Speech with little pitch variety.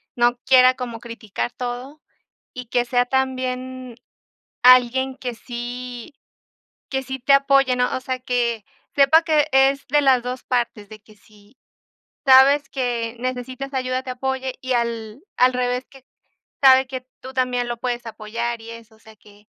Yes: narrow, 1.8 semitones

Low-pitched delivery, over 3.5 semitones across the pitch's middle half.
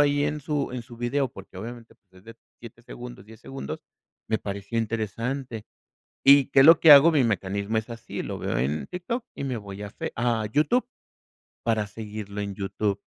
Yes: low, 115 Hz; average, 4.8 semitones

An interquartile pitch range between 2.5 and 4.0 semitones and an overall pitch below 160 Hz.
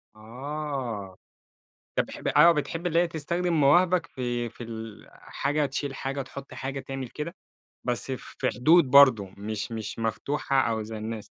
No: average, 4.7 semitones; low, 135 Hz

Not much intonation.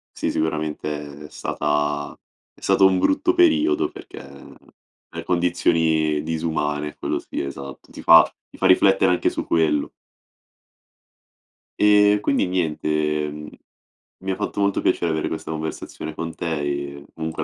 No: average, 4.0 semitones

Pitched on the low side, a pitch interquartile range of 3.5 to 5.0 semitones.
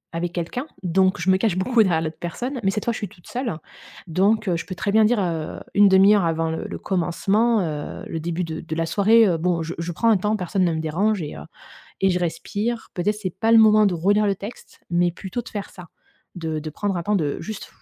No: medium, 185 Hz; average, 4.0 semitones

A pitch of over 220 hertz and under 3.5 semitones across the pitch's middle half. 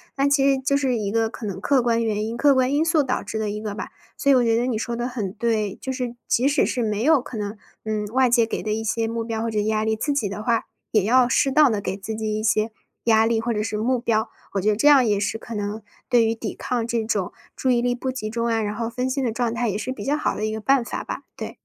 Yes: high, 230 Hz; average, 2.8 semitones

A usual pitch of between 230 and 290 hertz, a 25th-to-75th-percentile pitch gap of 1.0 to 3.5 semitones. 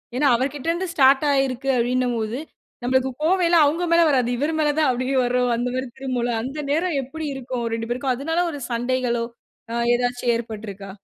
Yes: very high, 255 Hz; average, 3.2 semitones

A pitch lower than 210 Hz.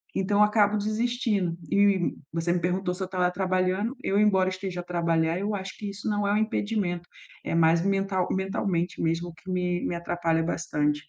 Yes: medium, 185 Hz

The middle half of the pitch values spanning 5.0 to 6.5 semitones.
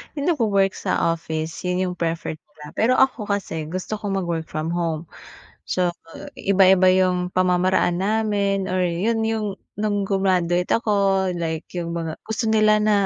No: average, 3.2 semitones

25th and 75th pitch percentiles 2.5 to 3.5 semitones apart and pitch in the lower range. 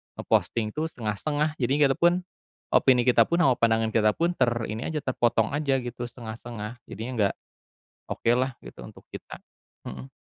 No: average, 4.6 semitones; low, 120 Hz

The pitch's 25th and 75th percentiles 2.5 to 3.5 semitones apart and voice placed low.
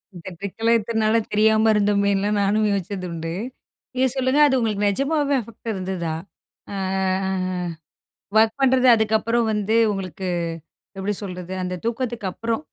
No: average, 2.9 semitones; high, 215 Hz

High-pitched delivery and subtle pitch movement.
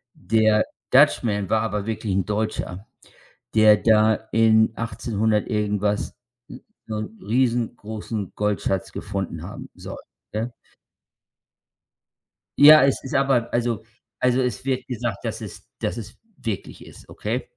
No: low, 110 Hz; narrow, 2.2 semitones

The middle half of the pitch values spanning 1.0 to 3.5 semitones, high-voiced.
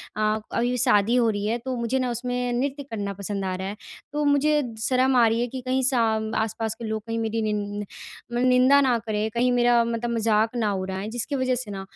Yes: average, 2.8 semitones; high, 230 Hz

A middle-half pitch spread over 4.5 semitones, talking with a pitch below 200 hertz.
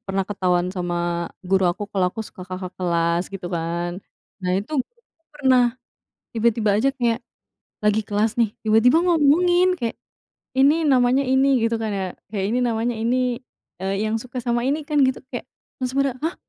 No: wide, 5.4 semitones; high, 230 Hz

